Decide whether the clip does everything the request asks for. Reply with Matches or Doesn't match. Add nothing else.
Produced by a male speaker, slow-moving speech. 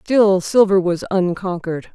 Doesn't match